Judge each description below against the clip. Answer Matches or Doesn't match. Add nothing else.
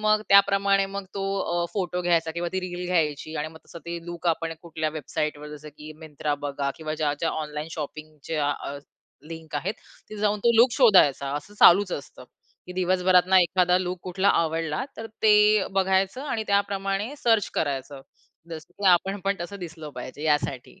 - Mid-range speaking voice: Matches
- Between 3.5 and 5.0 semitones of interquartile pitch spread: Matches